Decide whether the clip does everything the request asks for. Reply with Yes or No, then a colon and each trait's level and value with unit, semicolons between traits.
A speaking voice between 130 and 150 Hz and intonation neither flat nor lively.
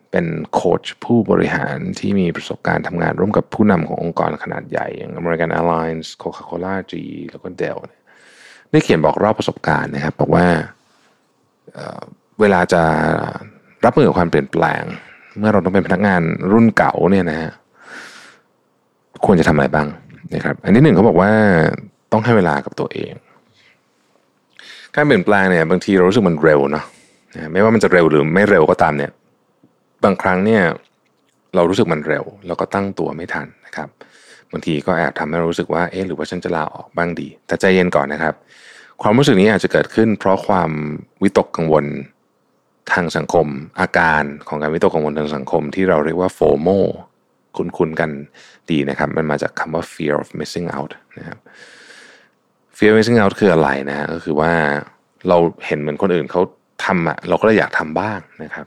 No: very low, 85 Hz; average, 3.8 semitones